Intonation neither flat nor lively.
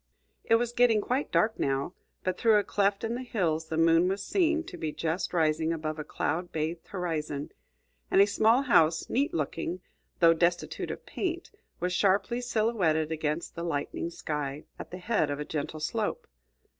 No: wide, 5.8 semitones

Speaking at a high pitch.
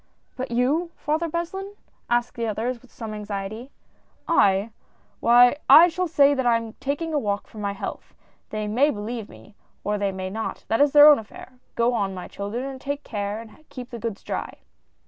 Yes: high, 235 Hz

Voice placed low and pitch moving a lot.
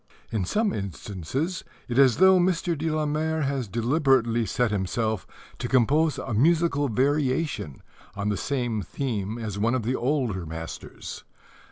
Yes: low, 130 Hz; wide, 5.8 semitones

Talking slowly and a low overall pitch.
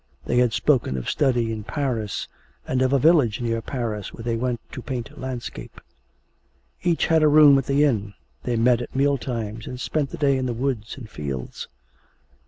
No: average, 190 wpm; low, 125 Hz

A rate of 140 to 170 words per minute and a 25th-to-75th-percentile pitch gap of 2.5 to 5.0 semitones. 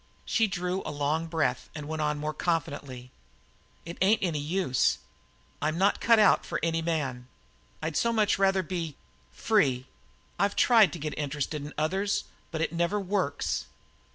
Yes: average, 160 wpm; average, 4.6 semitones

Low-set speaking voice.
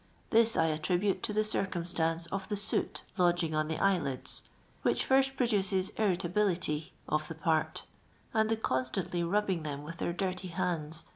No: medium, 180 Hz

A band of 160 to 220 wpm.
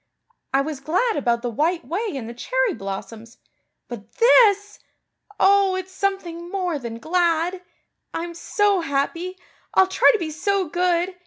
No: average, 150 wpm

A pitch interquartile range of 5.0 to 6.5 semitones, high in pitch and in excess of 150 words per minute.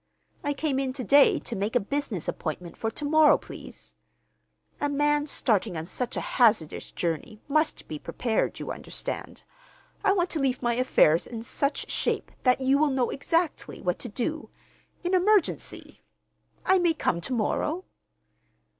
Yes: average, 5.3 semitones; very high, 265 Hz; average, 160 wpm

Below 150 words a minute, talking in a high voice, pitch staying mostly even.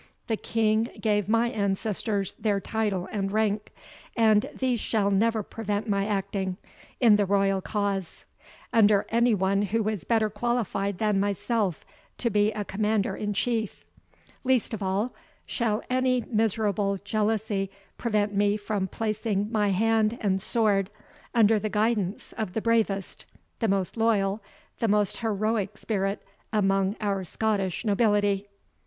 Yes: average, 140 wpm; high, 210 Hz; narrow, 2.0 semitones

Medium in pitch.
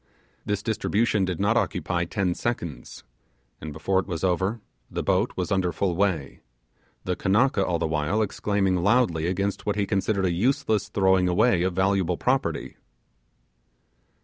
No: very low, 95 Hz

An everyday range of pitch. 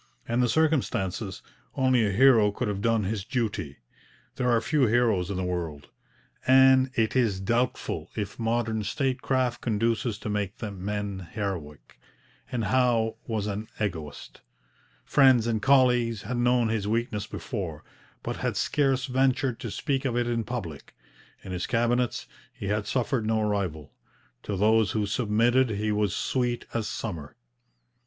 Yes: average, 3.5 semitones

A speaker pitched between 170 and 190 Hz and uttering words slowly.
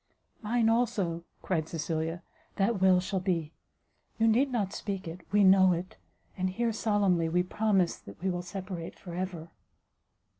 No: medium, 185 Hz; average, 155 wpm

